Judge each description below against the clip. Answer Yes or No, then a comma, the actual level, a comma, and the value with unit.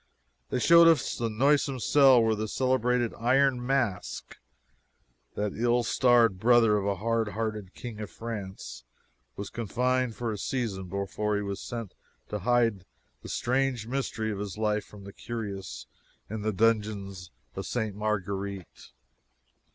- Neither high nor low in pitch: No, low, 110 Hz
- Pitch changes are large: No, average, 3.3 semitones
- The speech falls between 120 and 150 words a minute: Yes, average, 145 wpm